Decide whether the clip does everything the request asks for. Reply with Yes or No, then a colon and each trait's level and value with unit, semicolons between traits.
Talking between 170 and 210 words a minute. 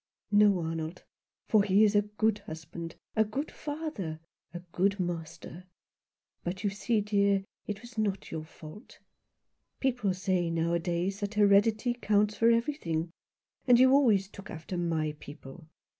No: average, 145 wpm